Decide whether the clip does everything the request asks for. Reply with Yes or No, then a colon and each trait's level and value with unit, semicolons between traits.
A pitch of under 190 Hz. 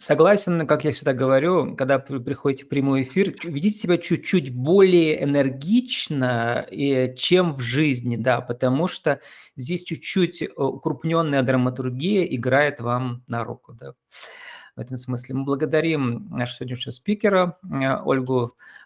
Yes: medium, 140 Hz